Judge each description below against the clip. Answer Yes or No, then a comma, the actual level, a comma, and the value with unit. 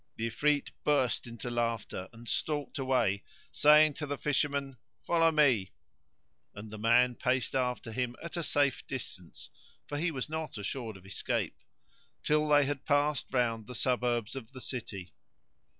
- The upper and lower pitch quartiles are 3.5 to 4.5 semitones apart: Yes, average, 4.1 semitones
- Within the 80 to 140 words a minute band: No, average, 155 wpm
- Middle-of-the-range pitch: No, low, 130 Hz